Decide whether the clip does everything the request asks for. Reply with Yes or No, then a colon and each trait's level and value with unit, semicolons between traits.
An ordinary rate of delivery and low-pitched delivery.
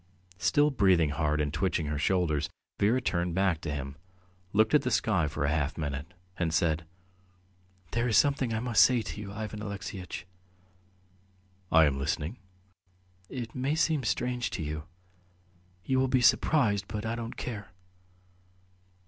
Yes: average, 160 wpm; very low, 95 Hz